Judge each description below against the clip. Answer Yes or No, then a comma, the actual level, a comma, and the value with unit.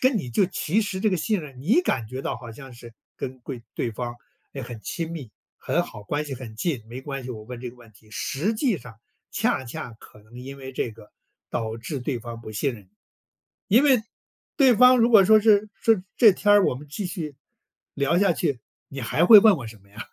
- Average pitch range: No, wide, 8.7 semitones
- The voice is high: No, low, 135 Hz